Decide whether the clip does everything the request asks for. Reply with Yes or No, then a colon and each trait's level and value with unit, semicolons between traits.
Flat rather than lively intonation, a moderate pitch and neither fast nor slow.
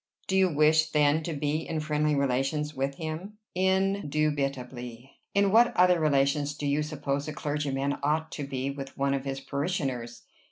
Yes: narrow, 2.3 semitones; medium, 145 Hz; average, 165 wpm